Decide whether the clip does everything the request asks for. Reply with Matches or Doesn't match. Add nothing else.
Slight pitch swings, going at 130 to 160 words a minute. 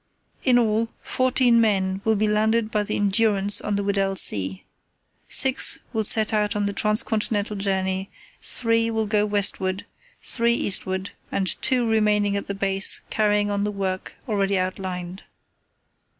Matches